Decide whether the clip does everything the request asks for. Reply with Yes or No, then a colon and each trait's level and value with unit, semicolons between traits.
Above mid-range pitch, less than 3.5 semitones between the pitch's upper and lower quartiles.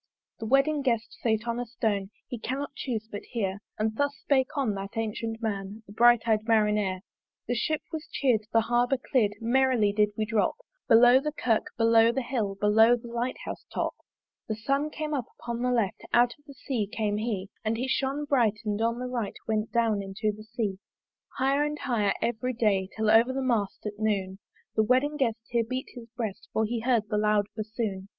Yes: high, 230 Hz; average, 2.9 semitones